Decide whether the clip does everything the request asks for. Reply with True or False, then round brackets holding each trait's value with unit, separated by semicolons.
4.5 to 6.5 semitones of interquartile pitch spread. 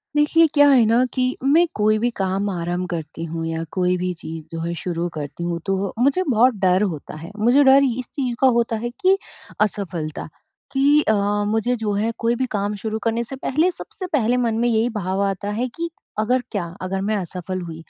True (5.4 semitones)